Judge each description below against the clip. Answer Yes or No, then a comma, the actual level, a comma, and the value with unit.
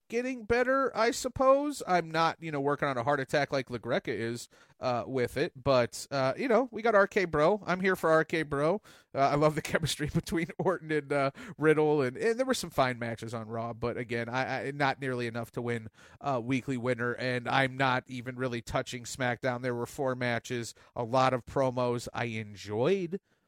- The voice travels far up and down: Yes, wide, 5.7 semitones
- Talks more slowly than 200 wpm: No, fast, 205 wpm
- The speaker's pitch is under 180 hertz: Yes, low, 135 Hz